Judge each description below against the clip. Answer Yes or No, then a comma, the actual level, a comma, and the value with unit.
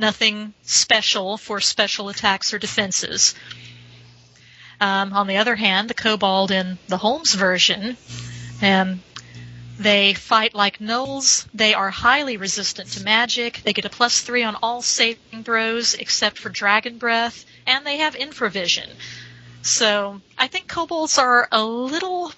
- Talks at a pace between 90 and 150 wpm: Yes, average, 140 wpm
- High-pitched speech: Yes, high, 215 Hz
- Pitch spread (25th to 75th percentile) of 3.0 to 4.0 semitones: Yes, average, 3.5 semitones